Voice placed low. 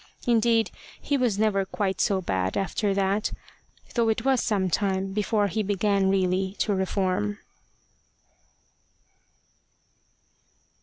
No: high, 200 Hz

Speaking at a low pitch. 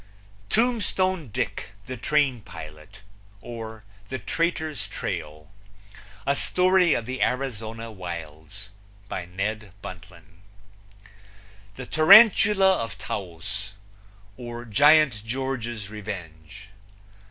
Yes: low, 110 Hz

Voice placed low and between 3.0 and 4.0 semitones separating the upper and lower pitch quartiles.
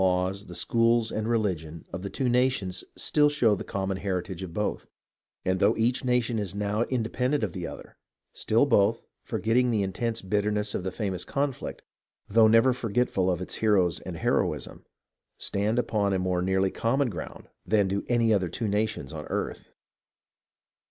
Yes: low, 105 Hz; average, 3.7 semitones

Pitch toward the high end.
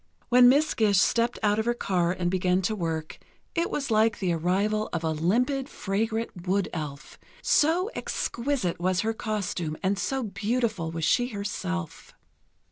Yes: high, 200 Hz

